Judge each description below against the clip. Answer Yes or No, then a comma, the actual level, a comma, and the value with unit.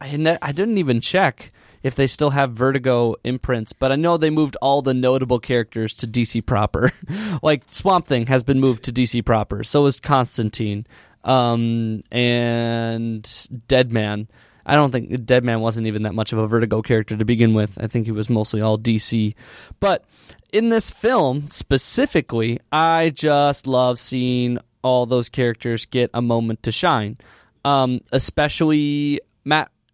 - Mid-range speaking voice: No, low, 125 Hz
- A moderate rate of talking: Yes, average, 160 wpm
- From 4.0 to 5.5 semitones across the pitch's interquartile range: No, average, 3.6 semitones